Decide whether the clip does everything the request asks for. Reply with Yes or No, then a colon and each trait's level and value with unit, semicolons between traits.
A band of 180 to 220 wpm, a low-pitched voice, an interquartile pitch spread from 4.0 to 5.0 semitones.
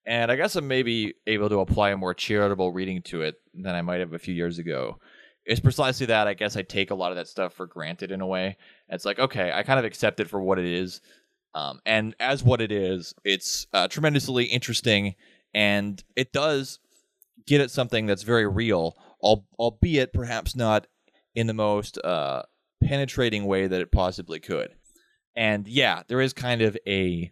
Yes: average, 200 wpm; low, 105 Hz; average, 4.5 semitones